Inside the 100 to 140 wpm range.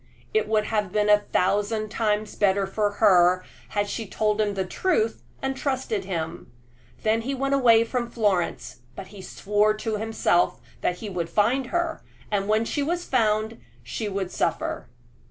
No: average, 170 wpm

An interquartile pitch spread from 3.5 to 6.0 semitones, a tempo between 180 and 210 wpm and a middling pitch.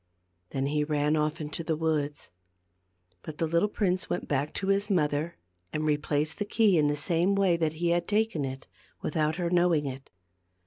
No: average, 3.1 semitones; average, 185 wpm; medium, 160 Hz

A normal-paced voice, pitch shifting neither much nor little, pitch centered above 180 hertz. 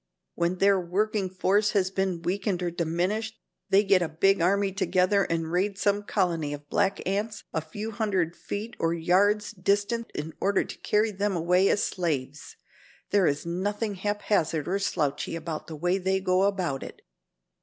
Yes: average, 170 wpm; average, 3.1 semitones; high, 190 Hz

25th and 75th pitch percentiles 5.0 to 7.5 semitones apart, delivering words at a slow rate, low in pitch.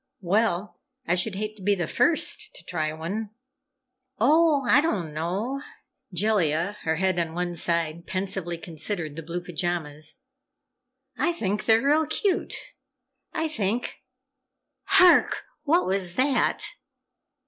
No: wide, 5.6 semitones; slow, 125 wpm; high, 190 Hz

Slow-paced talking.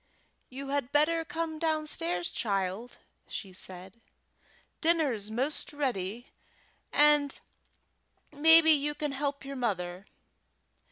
Yes: slow, 100 wpm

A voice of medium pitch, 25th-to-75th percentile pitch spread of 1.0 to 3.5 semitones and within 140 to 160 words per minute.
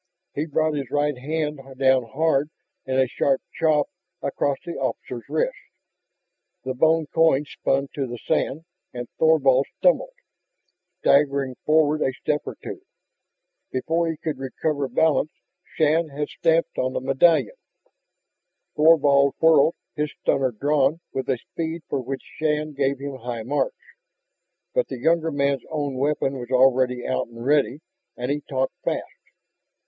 Yes: medium, 145 Hz; average, 3.0 semitones; average, 145 wpm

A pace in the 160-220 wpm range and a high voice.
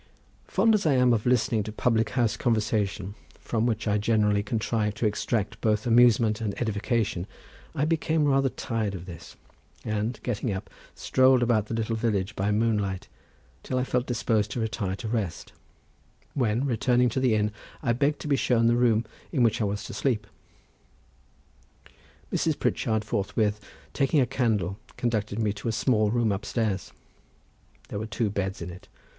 No: average, 170 wpm; low, 110 Hz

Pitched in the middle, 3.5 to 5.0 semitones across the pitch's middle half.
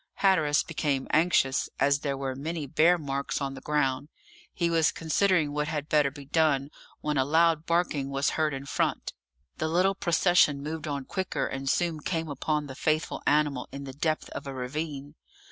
No: medium, 150 Hz; average, 2.7 semitones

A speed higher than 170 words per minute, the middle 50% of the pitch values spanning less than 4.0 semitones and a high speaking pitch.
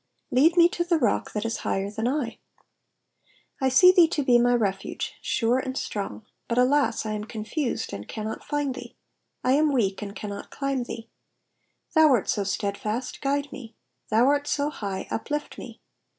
No: average, 180 wpm; average, 5.1 semitones; high, 245 Hz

